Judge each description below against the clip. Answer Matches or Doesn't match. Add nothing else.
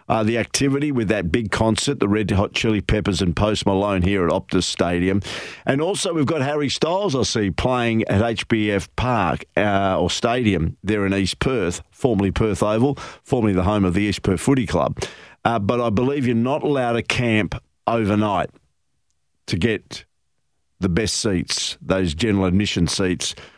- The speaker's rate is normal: Matches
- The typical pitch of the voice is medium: Doesn't match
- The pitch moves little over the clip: Doesn't match